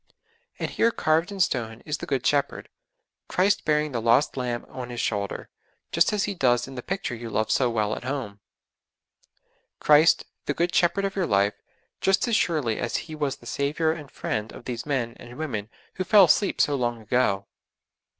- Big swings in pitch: Yes, wide, 5.8 semitones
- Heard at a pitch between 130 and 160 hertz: Yes, low, 135 Hz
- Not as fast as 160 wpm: No, average, 190 wpm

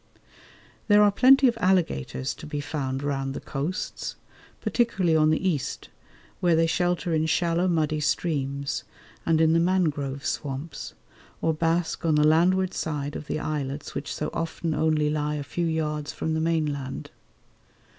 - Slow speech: No, average, 155 wpm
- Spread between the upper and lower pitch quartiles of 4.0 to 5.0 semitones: No, average, 2.8 semitones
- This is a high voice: No, medium, 155 Hz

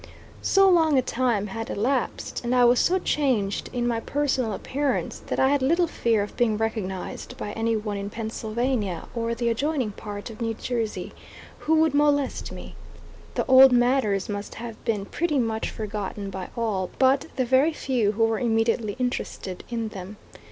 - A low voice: No, high, 230 Hz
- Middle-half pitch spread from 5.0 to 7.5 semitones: No, average, 3.7 semitones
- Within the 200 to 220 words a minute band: No, average, 175 wpm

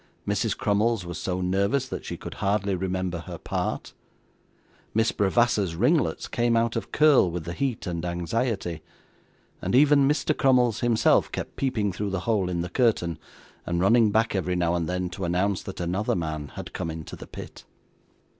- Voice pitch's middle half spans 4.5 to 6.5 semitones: Yes, average, 4.9 semitones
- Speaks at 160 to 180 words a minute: Yes, average, 175 wpm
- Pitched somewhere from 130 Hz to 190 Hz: No, low, 100 Hz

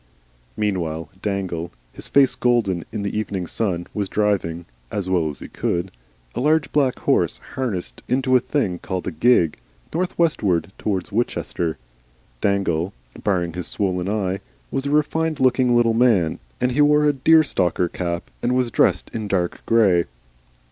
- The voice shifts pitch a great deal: Yes, wide, 6.1 semitones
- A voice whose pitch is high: No, low, 100 Hz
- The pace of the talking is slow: No, average, 155 wpm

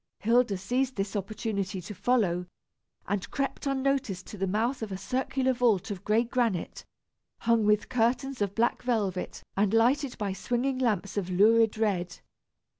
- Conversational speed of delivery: Yes, average, 155 wpm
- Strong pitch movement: No, average, 4.0 semitones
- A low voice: No, high, 220 Hz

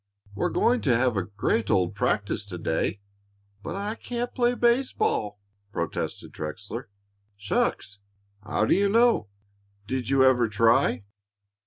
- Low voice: Yes, low, 115 Hz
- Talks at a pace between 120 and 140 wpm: Yes, slow, 135 wpm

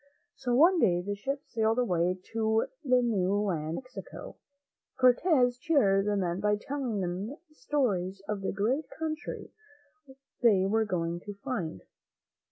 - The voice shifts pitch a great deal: No, average, 5.0 semitones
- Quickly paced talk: No, average, 145 wpm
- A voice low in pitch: No, high, 220 Hz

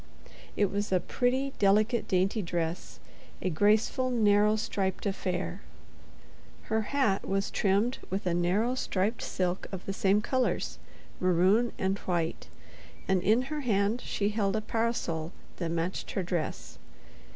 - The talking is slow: Yes, slow, 130 wpm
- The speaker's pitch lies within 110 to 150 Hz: No, high, 200 Hz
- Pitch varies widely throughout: No, average, 3.2 semitones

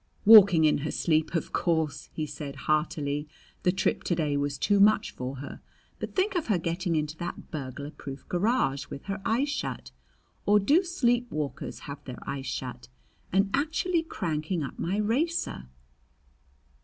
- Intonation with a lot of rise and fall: Yes, wide, 7.1 semitones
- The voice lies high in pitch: No, medium, 170 Hz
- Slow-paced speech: No, average, 165 wpm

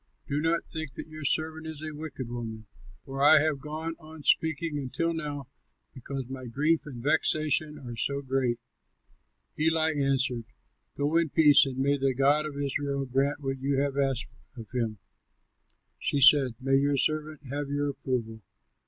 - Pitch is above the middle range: No, medium, 140 Hz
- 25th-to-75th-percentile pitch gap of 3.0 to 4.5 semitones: No, narrow, 2.5 semitones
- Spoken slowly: No, average, 165 wpm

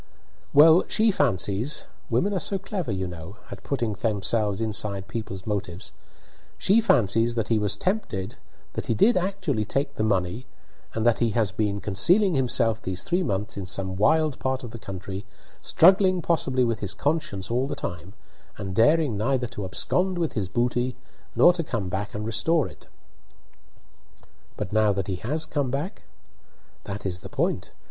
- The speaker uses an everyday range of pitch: No, wide, 7.2 semitones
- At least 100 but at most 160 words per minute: No, average, 170 wpm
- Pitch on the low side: Yes, low, 115 Hz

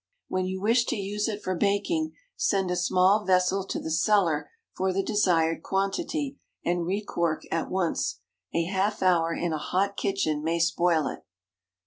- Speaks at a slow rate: No, average, 170 wpm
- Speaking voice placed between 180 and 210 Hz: Yes, medium, 185 Hz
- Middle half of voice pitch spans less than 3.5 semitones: Yes, average, 3.1 semitones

